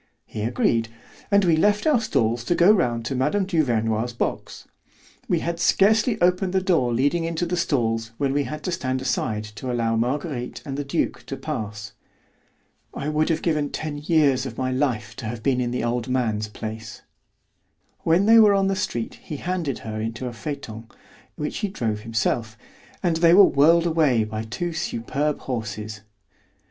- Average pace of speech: Yes, average, 180 wpm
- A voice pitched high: No, low, 135 Hz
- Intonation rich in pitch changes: Yes, wide, 6.7 semitones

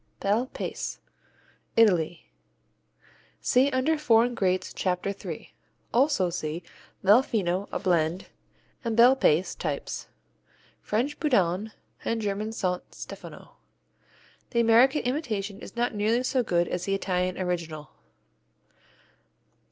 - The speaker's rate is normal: No, slow, 115 wpm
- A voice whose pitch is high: Yes, high, 205 Hz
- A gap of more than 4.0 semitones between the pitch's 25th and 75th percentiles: Yes, average, 5.1 semitones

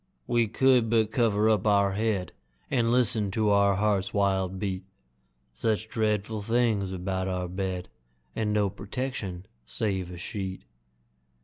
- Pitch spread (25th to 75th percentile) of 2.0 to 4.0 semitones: Yes, average, 2.7 semitones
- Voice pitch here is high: No, low, 100 Hz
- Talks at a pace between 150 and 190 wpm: No, slow, 135 wpm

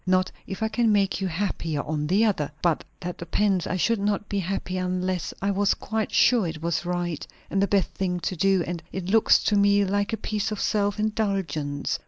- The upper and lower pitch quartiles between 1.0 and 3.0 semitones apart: Yes, narrow, 2.6 semitones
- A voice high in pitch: Yes, high, 195 Hz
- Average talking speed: No, fast, 215 wpm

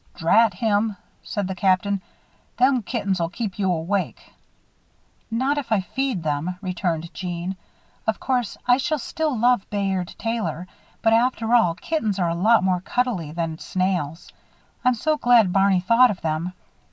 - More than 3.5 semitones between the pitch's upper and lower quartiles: Yes, average, 4.8 semitones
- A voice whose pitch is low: No, high, 200 Hz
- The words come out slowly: No, average, 155 wpm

